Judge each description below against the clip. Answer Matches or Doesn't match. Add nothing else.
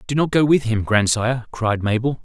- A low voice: Matches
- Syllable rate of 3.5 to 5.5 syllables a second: Matches